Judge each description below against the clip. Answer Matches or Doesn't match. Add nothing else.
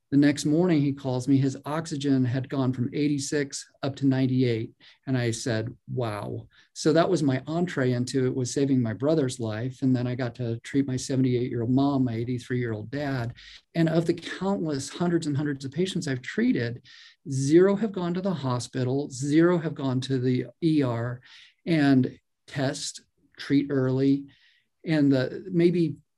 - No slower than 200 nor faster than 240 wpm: Doesn't match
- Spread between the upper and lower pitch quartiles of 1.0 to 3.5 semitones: Matches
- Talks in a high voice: Doesn't match